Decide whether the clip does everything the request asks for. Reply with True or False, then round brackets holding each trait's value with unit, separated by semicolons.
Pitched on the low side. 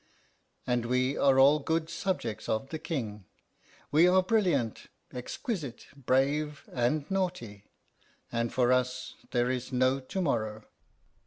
True (130 Hz)